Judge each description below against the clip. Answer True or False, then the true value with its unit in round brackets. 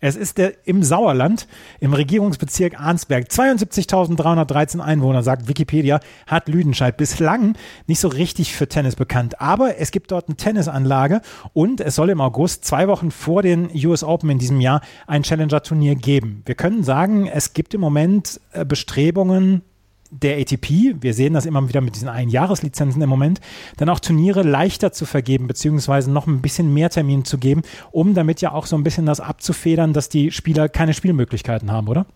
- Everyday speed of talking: True (175 wpm)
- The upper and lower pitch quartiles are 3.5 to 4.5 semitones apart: True (4.0 semitones)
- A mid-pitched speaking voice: True (155 Hz)